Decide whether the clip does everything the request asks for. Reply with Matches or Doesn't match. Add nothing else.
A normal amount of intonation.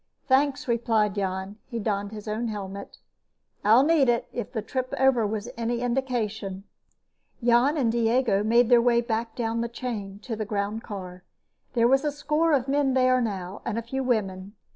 Matches